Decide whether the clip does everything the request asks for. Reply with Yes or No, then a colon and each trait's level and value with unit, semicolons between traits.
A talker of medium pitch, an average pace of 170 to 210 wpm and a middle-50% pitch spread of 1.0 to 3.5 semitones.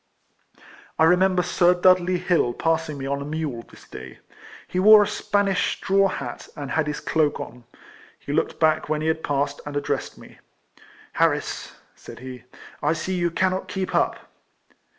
No: medium, 160 Hz; average, 175 wpm; average, 4.3 semitones